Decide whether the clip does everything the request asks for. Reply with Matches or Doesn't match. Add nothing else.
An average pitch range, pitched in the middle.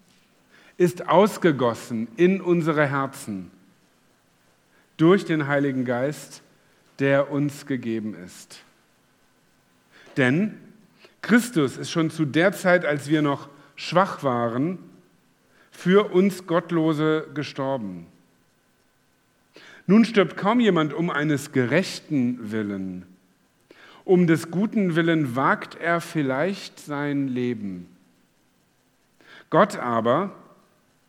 Doesn't match